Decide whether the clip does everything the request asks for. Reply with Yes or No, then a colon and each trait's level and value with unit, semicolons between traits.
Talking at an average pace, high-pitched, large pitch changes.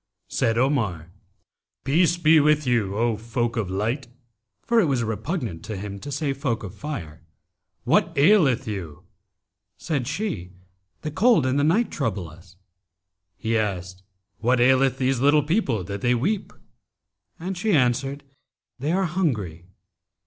No: average, 145 wpm; low, 125 Hz; wide, 6.7 semitones